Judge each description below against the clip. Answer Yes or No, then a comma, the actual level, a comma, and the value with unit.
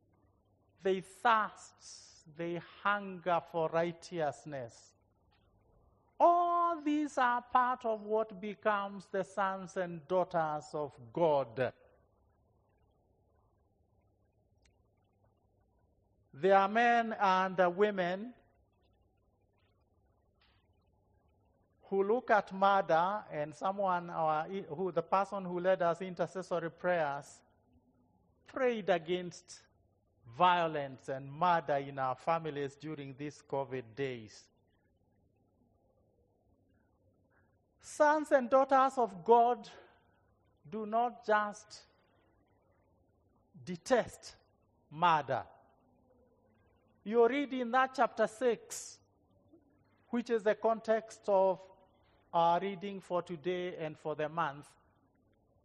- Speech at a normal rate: No, slow, 85 wpm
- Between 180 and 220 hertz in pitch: No, medium, 160 Hz